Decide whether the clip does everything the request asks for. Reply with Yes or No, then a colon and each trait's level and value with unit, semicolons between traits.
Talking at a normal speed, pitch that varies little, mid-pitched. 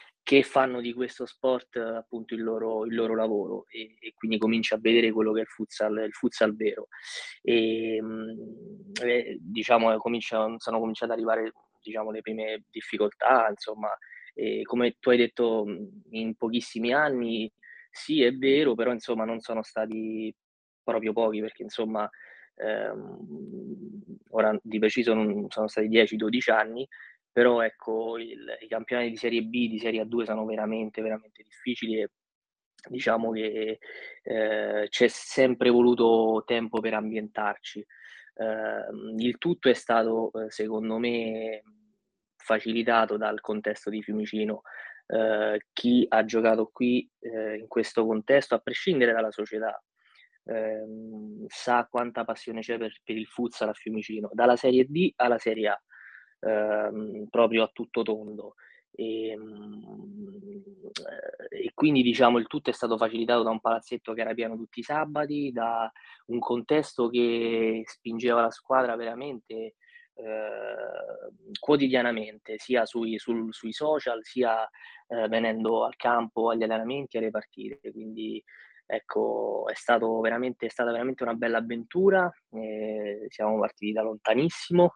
No: average, 135 wpm; narrow, 1.8 semitones; low, 115 Hz